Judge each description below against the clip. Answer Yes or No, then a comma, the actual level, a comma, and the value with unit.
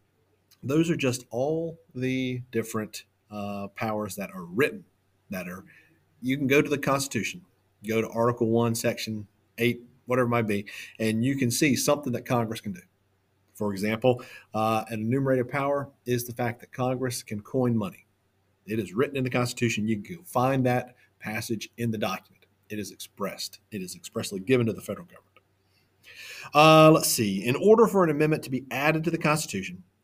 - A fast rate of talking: No, average, 180 wpm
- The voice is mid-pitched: No, low, 120 Hz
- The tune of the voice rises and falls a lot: No, average, 3.9 semitones